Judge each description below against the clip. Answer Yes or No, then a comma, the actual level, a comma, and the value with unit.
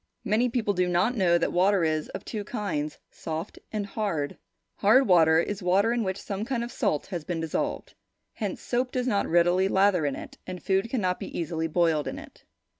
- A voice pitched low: No, high, 190 Hz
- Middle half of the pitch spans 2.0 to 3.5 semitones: No, average, 4.3 semitones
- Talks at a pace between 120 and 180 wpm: No, average, 200 wpm